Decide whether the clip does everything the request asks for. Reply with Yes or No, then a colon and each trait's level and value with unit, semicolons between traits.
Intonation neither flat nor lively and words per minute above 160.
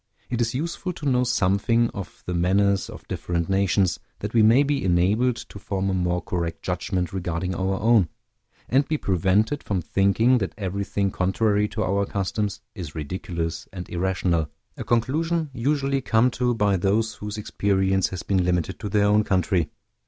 Yes: average, 3.9 semitones; average, 170 wpm